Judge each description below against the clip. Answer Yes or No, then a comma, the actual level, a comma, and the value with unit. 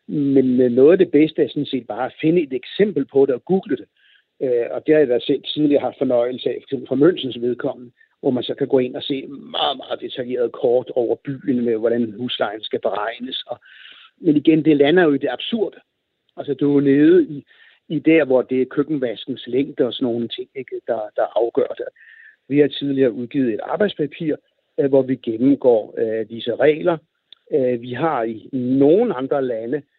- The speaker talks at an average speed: Yes, average, 200 wpm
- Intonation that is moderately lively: No, wide, 5.7 semitones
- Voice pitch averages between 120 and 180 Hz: Yes, medium, 140 Hz